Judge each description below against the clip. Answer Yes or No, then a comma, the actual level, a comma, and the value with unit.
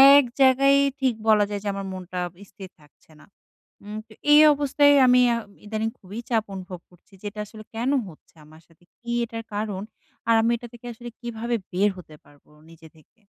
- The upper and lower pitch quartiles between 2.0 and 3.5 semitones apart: No, average, 4.3 semitones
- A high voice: Yes, high, 215 Hz